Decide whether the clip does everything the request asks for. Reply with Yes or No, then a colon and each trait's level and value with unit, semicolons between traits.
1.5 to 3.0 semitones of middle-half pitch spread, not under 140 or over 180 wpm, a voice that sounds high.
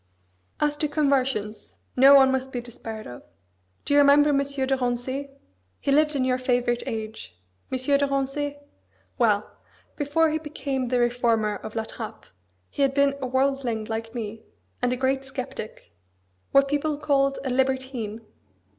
Yes: narrow, 2.6 semitones; average, 155 wpm; very high, 265 Hz